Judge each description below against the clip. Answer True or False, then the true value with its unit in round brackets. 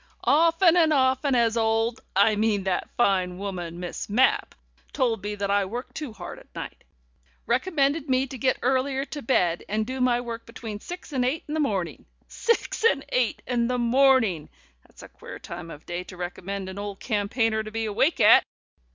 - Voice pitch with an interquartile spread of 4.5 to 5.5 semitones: True (4.8 semitones)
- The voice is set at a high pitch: True (230 Hz)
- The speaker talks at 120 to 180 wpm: False (195 wpm)